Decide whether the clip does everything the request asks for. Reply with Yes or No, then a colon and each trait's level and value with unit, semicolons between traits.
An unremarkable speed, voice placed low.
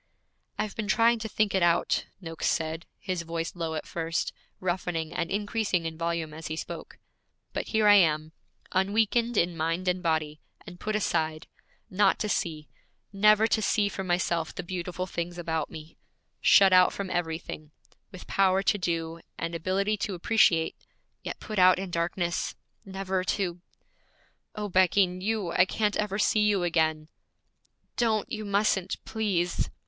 No: average, 160 wpm; medium, 180 Hz